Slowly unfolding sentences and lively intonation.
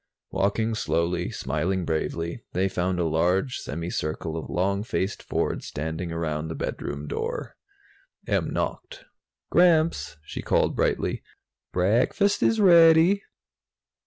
Yes: slow, 130 wpm; wide, 6.3 semitones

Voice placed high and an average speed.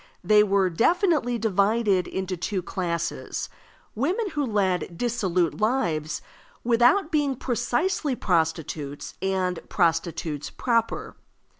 No: high, 205 Hz; slow, 100 wpm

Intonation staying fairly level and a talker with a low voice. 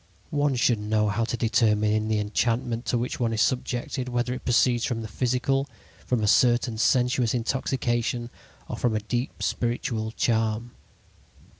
Yes: narrow, 2.2 semitones; low, 120 Hz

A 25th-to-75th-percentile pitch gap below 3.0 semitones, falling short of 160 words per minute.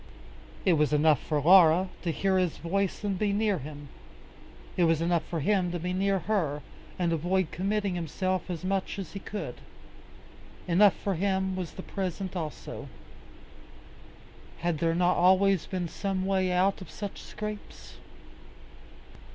Yes: narrow, 2.6 semitones; average, 150 wpm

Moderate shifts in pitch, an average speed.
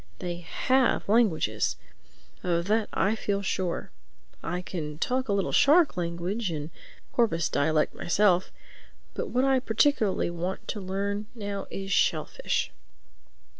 No: average, 4.4 semitones; slow, 130 wpm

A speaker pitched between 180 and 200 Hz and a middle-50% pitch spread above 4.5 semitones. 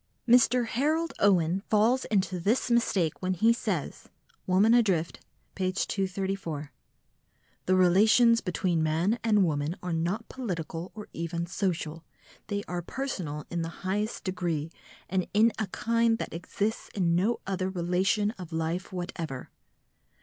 No: medium, 185 Hz; average, 4.2 semitones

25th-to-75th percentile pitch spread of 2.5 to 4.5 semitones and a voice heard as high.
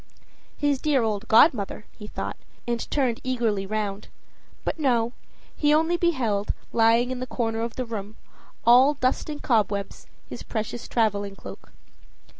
Yes: average, 3.4 semitones; high, 235 Hz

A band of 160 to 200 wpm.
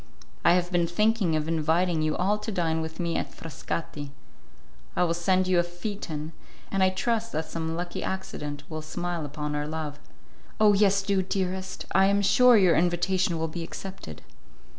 Yes: average, 180 wpm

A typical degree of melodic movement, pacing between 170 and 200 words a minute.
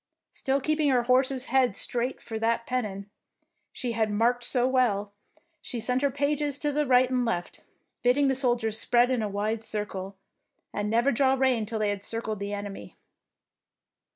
Yes: average, 3.5 semitones; average, 180 wpm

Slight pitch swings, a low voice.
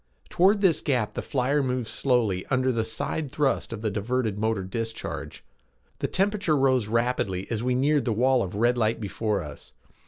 No: average, 3.6 semitones; low, 120 Hz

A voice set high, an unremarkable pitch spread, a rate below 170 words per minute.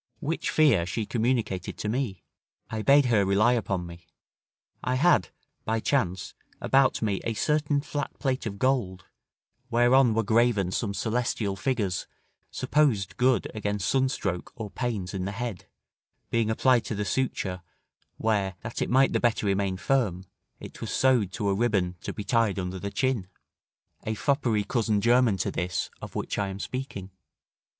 No: low, 110 Hz; average, 4.5 semitones; average, 160 wpm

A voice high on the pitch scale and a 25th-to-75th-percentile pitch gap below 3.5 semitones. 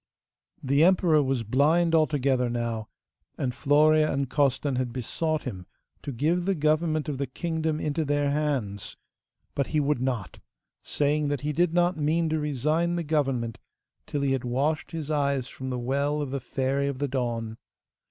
No: medium, 145 Hz; average, 3.1 semitones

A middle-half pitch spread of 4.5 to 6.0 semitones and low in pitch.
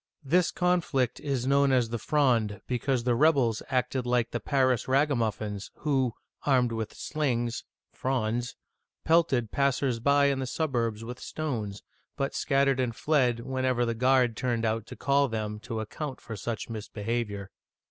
No: average, 3.2 semitones; low, 125 Hz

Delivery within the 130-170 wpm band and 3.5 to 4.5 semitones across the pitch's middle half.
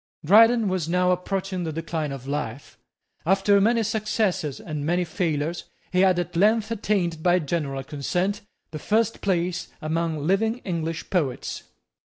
Yes: average, 145 wpm; average, 4.0 semitones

